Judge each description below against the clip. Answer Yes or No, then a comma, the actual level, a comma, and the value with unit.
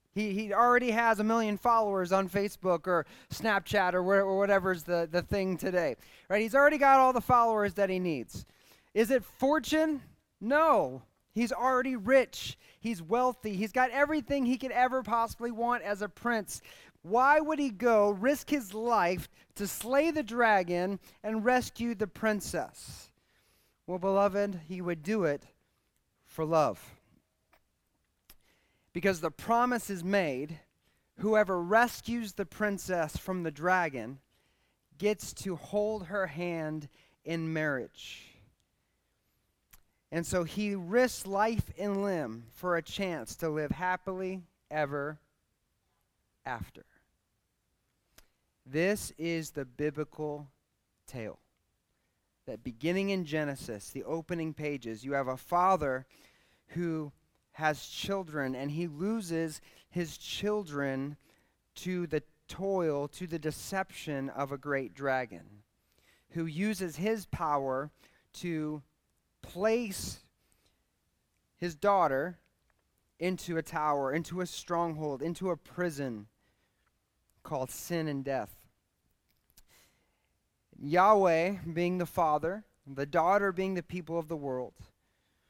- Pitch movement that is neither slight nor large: No, wide, 5.8 semitones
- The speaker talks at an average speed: No, slow, 120 wpm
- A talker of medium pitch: Yes, medium, 180 Hz